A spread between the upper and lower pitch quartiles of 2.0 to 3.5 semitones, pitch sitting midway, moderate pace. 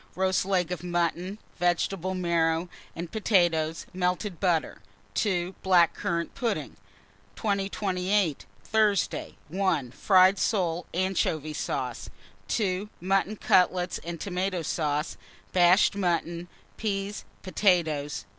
No: narrow, 2.5 semitones; medium, 180 Hz; slow, 100 wpm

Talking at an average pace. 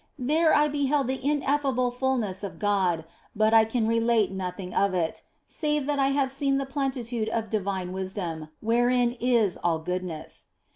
Yes: average, 160 wpm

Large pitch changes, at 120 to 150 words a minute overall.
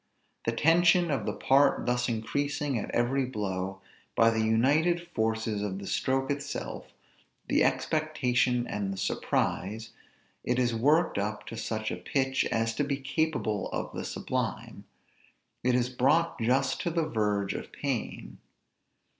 No: average, 4.5 semitones; average, 145 wpm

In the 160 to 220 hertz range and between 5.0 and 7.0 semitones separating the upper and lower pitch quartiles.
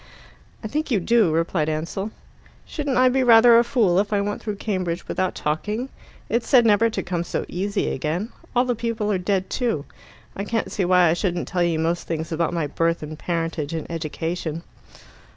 Yes: medium, 185 Hz; average, 5.3 semitones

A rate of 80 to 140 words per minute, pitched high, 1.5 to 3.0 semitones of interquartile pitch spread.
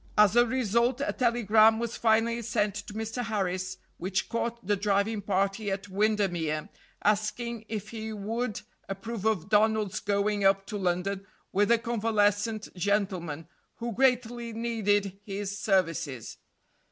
Yes: slow, 135 wpm; high, 210 Hz; narrow, 2.5 semitones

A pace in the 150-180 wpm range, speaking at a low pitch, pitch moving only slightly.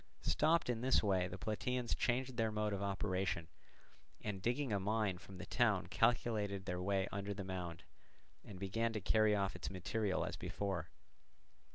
No: average, 170 wpm; low, 100 Hz; average, 3.0 semitones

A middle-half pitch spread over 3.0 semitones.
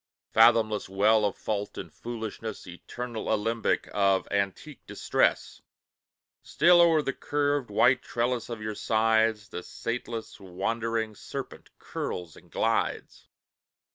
No: narrow, 2.6 semitones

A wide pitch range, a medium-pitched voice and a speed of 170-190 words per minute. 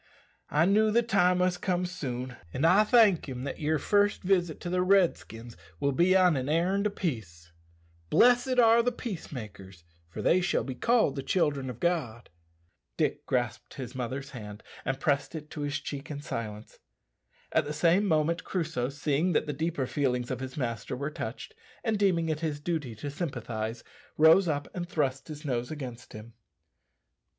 Yes: wide, 5.9 semitones; medium, 150 Hz; average, 180 wpm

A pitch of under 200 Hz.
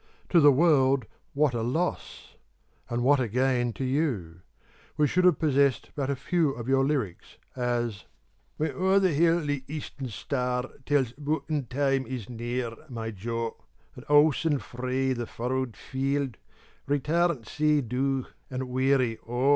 Yes: low, 135 Hz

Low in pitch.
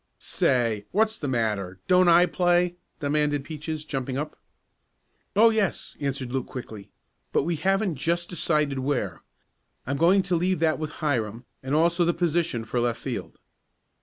No: medium, 150 Hz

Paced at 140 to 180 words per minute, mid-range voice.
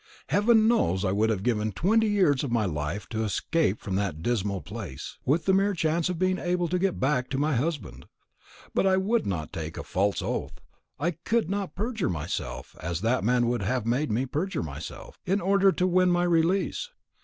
No: average, 200 wpm; medium, 145 Hz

